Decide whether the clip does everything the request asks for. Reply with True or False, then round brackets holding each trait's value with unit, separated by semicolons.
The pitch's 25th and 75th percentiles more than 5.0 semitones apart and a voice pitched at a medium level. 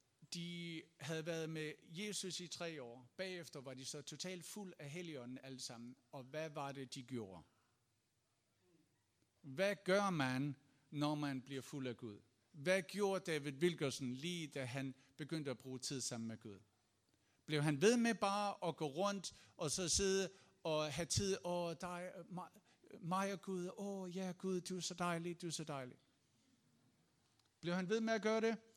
True (5.5 semitones; 155 Hz)